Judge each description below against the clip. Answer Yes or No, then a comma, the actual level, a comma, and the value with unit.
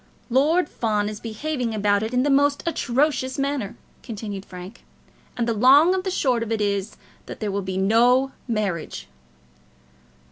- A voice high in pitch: Yes, high, 230 Hz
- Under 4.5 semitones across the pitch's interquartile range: No, average, 4.9 semitones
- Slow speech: No, average, 165 wpm